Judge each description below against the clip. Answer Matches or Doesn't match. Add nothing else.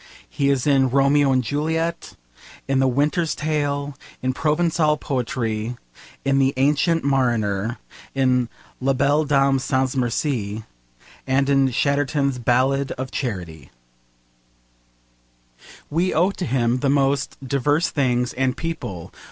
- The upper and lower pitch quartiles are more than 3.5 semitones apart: Doesn't match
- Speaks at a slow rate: Matches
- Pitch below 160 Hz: Matches